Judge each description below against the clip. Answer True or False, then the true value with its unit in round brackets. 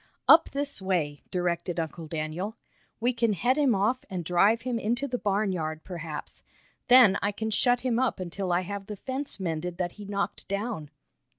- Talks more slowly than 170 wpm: False (180 wpm)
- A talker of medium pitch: False (200 Hz)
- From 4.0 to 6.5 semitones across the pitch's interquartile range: True (5.4 semitones)